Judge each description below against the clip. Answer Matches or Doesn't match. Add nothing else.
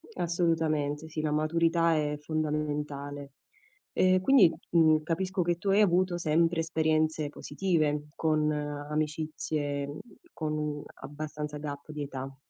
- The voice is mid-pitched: Matches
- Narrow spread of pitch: Matches